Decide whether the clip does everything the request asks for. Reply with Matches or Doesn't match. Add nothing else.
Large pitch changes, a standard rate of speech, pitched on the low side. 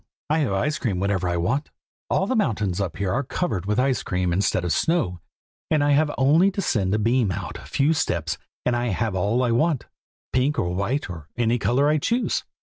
Doesn't match